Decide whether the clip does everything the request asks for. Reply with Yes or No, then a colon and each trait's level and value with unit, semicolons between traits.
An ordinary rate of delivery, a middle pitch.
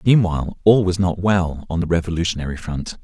No: average, 180 wpm; very low, 90 Hz